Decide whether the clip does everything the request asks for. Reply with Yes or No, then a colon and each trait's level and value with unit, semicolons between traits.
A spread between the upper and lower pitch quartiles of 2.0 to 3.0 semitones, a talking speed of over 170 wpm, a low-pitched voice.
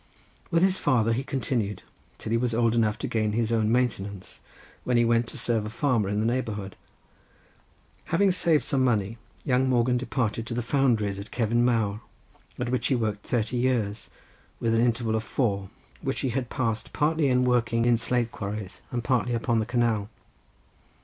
Yes: narrow, 2.5 semitones; average, 180 wpm; low, 115 Hz